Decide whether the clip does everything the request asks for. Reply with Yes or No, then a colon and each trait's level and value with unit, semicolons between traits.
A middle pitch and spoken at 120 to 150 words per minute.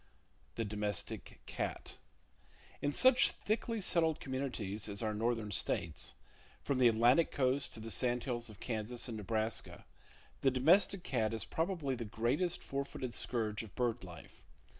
No: low, 120 Hz; average, 145 wpm